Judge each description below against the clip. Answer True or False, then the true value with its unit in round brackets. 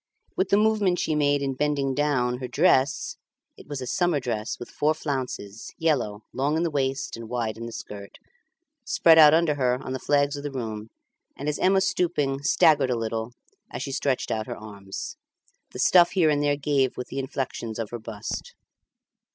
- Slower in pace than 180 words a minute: False (195 wpm)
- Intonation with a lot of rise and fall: False (3.9 semitones)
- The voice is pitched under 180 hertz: True (135 Hz)